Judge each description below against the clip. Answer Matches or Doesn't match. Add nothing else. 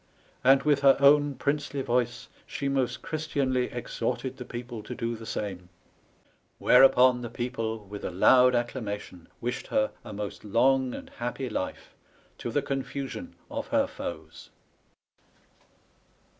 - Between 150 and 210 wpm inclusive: Doesn't match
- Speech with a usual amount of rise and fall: Matches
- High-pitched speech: Doesn't match